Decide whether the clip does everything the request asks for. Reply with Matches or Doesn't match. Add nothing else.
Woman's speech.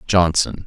Doesn't match